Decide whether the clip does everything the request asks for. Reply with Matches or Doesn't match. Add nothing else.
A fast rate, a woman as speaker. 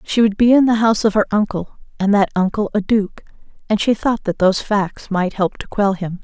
Matches